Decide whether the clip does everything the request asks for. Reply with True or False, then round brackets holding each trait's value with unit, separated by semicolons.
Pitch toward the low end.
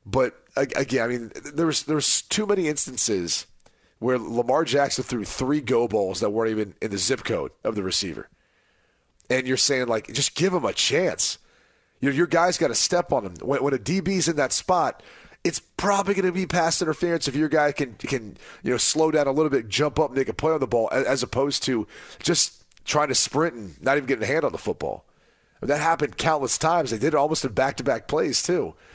False (145 Hz)